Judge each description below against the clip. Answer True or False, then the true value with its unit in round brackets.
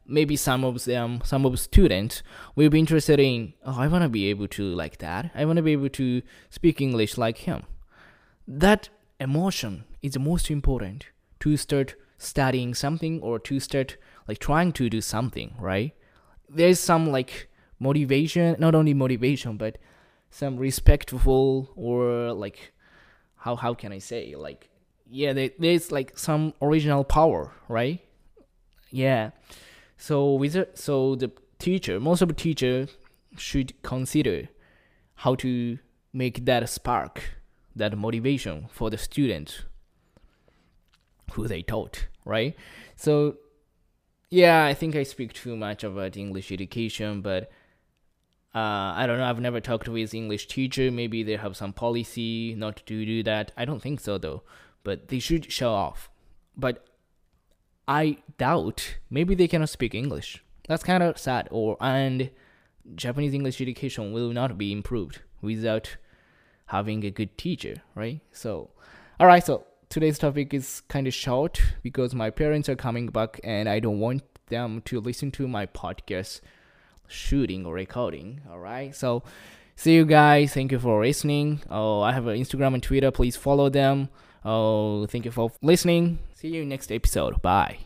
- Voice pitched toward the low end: True (130 Hz)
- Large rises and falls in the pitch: False (4.5 semitones)